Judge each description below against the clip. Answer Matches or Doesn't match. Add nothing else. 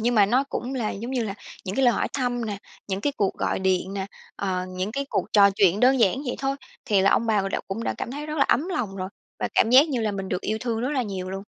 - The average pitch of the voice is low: Doesn't match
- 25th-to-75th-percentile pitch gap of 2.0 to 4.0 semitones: Doesn't match